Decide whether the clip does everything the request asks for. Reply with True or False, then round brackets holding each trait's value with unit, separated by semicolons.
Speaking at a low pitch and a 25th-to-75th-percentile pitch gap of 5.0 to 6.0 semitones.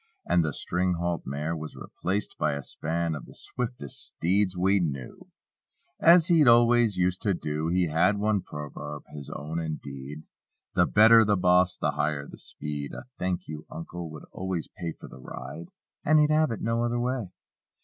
True (90 Hz; 5.6 semitones)